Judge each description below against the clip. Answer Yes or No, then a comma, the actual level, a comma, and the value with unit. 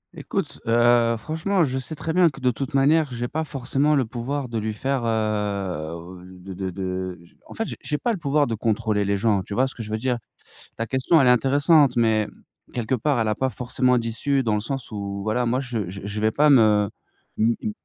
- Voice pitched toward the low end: Yes, low, 120 Hz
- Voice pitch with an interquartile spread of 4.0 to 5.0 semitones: Yes, average, 4.4 semitones